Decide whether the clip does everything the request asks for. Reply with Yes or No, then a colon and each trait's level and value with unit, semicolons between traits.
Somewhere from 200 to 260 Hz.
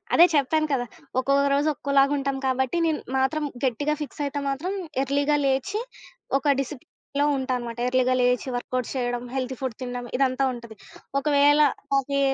No: very high, 270 Hz